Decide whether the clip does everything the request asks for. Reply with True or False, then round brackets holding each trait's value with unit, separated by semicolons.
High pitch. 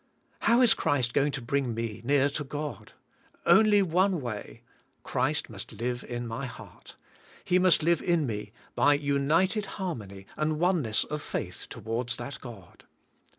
False (140 Hz)